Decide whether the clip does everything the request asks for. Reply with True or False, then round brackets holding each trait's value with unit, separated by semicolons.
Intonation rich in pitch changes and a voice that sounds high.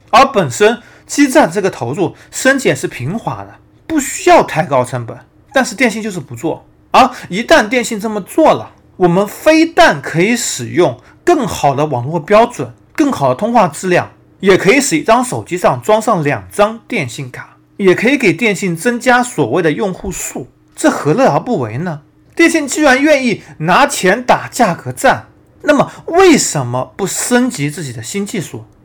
True (9.0 semitones; 210 Hz)